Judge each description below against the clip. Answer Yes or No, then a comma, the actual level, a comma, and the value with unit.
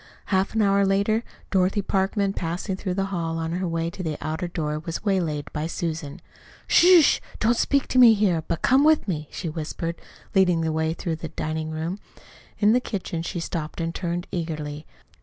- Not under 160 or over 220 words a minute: Yes, average, 180 wpm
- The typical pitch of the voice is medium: Yes, medium, 175 Hz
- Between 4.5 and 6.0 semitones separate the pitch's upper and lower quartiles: No, average, 3.5 semitones